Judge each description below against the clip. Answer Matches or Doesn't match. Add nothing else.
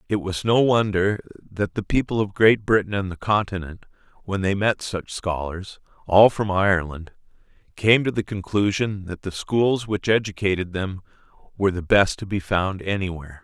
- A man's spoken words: Matches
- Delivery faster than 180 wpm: Doesn't match